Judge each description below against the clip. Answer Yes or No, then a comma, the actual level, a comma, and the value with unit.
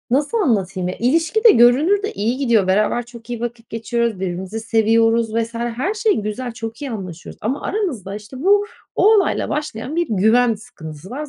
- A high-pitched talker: Yes, high, 235 Hz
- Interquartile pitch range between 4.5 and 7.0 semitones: Yes, average, 4.8 semitones